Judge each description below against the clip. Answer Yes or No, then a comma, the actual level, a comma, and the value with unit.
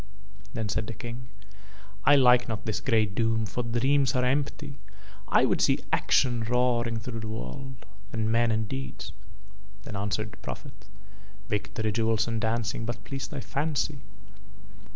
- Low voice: Yes, low, 115 Hz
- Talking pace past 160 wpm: No, average, 155 wpm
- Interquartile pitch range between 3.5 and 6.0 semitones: No, narrow, 2.4 semitones